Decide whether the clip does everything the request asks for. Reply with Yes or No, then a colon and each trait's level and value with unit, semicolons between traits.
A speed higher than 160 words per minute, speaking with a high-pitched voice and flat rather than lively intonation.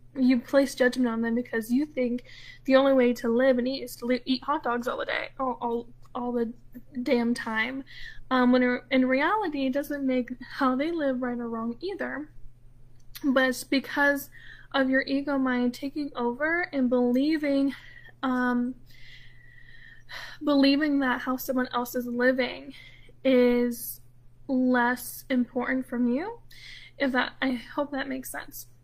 No: average, 155 wpm; very high, 255 Hz; narrow, 2.0 semitones